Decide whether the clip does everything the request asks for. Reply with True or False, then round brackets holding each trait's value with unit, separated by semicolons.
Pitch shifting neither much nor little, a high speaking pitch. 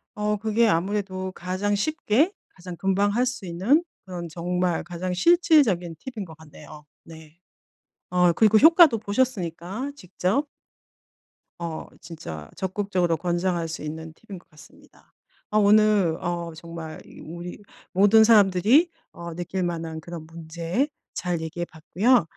False (4.0 semitones; 180 Hz)